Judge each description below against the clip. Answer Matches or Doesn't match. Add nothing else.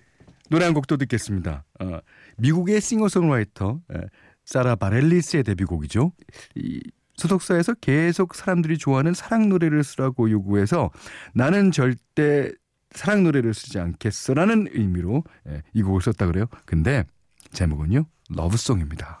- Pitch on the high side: Doesn't match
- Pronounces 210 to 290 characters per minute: Doesn't match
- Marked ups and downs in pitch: Matches